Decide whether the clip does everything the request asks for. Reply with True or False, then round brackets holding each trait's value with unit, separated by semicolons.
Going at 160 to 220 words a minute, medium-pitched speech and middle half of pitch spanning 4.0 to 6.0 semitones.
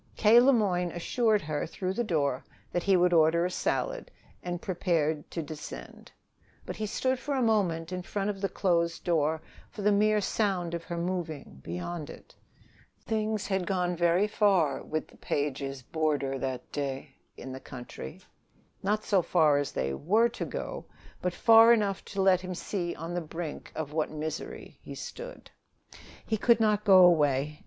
True (175 wpm; 175 Hz; 4.9 semitones)